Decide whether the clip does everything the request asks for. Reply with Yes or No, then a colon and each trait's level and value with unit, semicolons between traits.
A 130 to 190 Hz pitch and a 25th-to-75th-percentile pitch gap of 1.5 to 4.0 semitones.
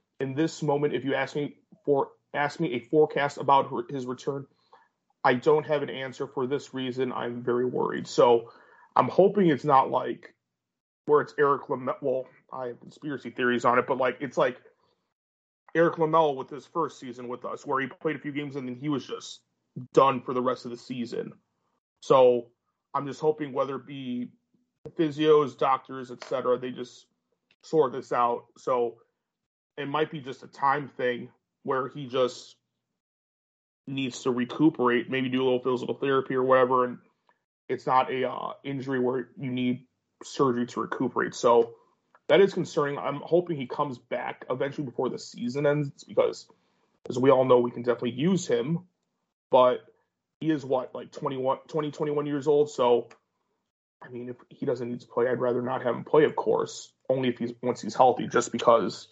Yes: low, 135 Hz; average, 3.5 semitones